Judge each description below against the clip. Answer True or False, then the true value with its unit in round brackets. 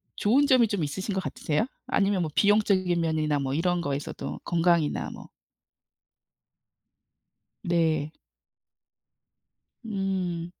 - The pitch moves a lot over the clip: False (4.0 semitones)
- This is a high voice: False (175 Hz)